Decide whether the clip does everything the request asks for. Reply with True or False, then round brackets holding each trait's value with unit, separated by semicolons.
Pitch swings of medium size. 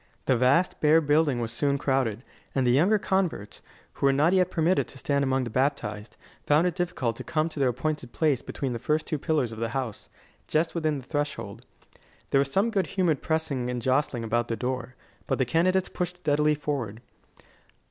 True (4.2 semitones)